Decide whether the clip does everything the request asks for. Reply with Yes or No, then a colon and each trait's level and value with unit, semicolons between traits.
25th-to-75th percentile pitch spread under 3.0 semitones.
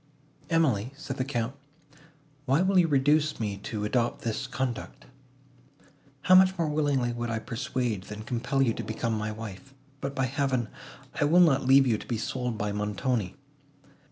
No: average, 3.8 semitones